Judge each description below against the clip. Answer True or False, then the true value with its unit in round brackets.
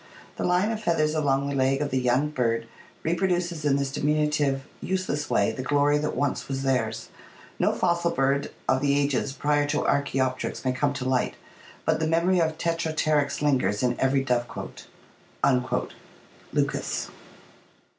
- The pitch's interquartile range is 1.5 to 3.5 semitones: True (2.8 semitones)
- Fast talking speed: False (155 wpm)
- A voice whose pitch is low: False (145 Hz)